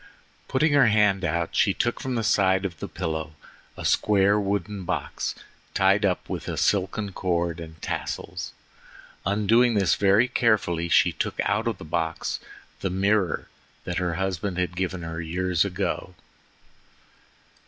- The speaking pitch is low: Yes, very low, 95 Hz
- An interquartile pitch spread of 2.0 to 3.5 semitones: Yes, average, 3.1 semitones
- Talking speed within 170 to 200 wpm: No, average, 150 wpm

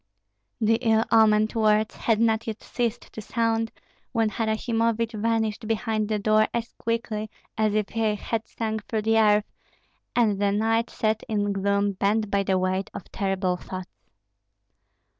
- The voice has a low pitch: No, high, 220 Hz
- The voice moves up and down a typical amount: No, narrow, 1.5 semitones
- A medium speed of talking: Yes, average, 155 wpm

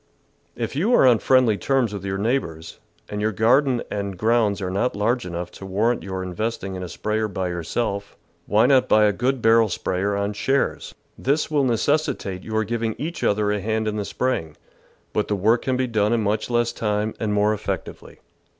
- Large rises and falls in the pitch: No, average, 3.1 semitones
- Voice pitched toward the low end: Yes, low, 110 Hz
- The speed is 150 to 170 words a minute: No, average, 200 wpm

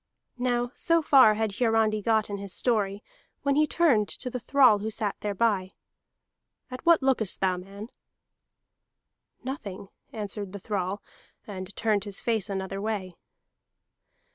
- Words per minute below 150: Yes, average, 140 wpm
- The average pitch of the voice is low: No, high, 215 Hz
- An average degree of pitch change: Yes, average, 3.5 semitones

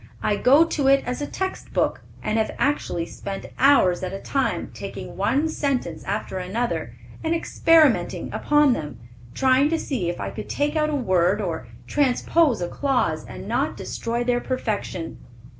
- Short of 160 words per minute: No, average, 170 wpm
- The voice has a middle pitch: No, very high, 250 Hz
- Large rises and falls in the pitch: Yes, wide, 6.9 semitones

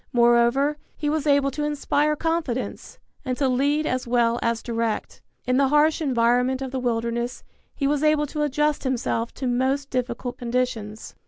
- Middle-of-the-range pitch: No, very high, 260 Hz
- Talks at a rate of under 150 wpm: No, average, 165 wpm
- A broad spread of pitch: No, average, 3.6 semitones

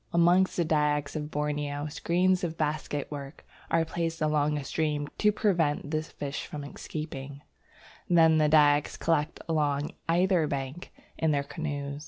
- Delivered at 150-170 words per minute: No, average, 140 wpm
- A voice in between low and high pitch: Yes, medium, 150 Hz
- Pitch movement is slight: Yes, narrow, 2.2 semitones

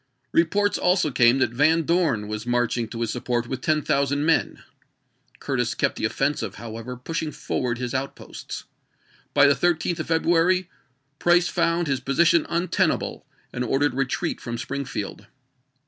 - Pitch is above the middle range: No, medium, 140 Hz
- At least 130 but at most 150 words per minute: No, average, 160 wpm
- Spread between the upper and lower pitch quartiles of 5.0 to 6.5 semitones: Yes, average, 5.3 semitones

